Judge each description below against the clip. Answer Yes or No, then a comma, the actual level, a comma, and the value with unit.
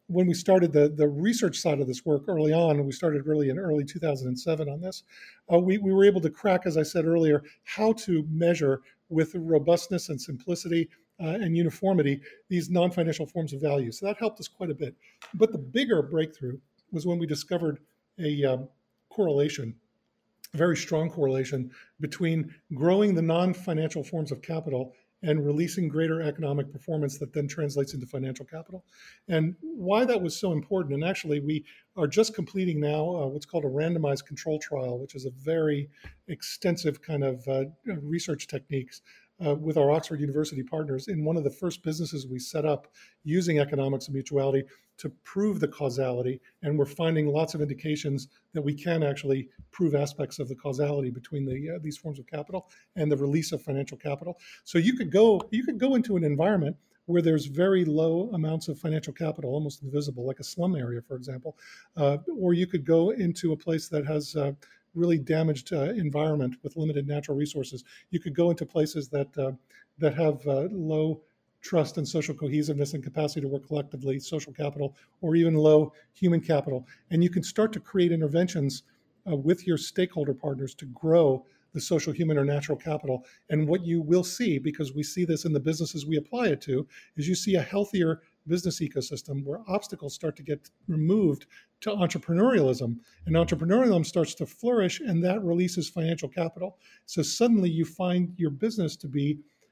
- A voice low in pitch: No, medium, 155 Hz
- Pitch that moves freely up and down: No, average, 3.2 semitones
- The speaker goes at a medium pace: Yes, average, 185 wpm